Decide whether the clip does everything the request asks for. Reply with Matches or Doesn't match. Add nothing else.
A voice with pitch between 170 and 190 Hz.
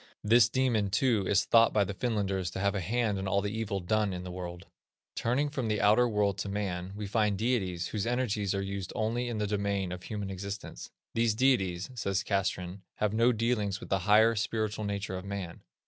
Doesn't match